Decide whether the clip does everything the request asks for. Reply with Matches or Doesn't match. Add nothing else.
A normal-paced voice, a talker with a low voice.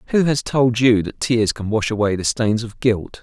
Doesn't match